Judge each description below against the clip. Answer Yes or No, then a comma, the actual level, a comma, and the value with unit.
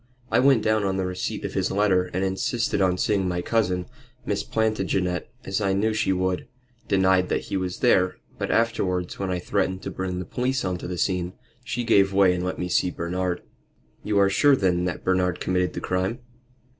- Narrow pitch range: Yes, narrow, 2.1 semitones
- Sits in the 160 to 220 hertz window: No, very low, 95 Hz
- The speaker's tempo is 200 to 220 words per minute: Yes, fast, 205 wpm